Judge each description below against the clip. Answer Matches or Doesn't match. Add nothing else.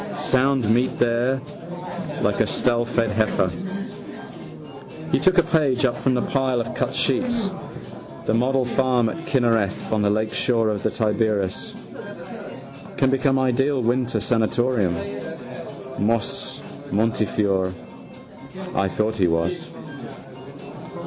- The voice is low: Matches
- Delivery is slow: Matches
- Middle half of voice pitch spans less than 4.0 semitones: Matches